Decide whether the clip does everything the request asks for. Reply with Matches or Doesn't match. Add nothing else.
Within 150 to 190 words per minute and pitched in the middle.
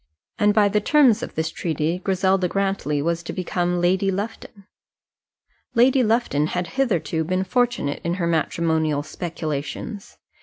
Doesn't match